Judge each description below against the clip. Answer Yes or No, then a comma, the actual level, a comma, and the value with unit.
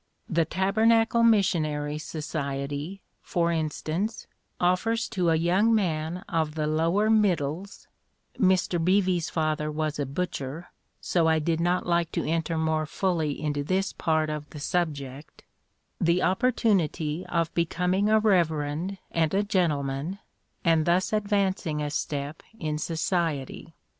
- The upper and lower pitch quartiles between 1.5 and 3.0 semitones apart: No, average, 3.5 semitones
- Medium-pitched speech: Yes, medium, 165 Hz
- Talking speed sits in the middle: No, slow, 130 wpm